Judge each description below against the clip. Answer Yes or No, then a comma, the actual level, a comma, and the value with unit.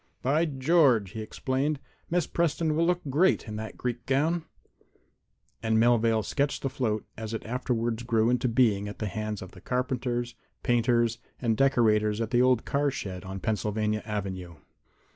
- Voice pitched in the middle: No, low, 120 Hz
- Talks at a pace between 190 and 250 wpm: No, average, 160 wpm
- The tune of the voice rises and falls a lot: No, average, 3.7 semitones